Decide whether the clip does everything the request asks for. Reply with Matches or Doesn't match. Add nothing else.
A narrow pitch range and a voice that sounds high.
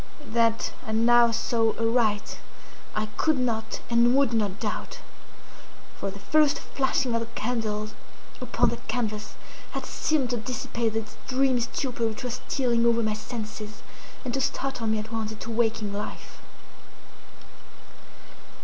Matches